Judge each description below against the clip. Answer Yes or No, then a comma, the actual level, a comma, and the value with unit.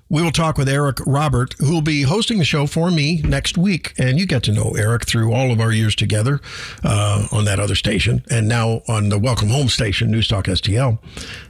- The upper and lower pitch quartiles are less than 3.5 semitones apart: No, average, 4.8 semitones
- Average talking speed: No, fast, 220 wpm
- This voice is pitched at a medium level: No, low, 125 Hz